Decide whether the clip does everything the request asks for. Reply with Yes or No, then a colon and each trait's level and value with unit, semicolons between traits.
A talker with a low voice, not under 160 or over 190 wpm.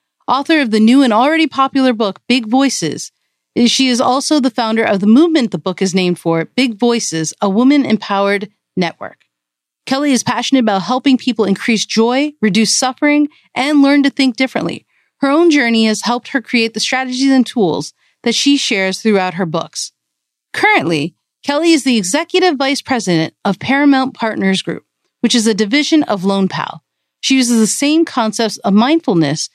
No: high, 240 Hz; average, 175 wpm